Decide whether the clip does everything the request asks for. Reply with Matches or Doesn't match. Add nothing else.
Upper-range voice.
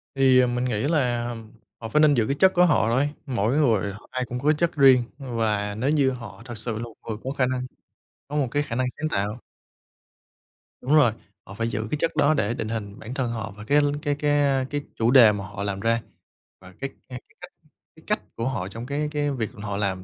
Doesn't match